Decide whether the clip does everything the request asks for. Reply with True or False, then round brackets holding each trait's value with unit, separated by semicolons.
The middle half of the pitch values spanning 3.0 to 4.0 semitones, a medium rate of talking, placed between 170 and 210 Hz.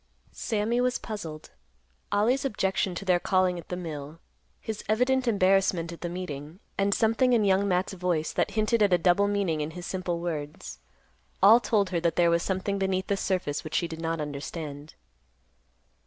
True (3.4 semitones; 180 wpm; 185 Hz)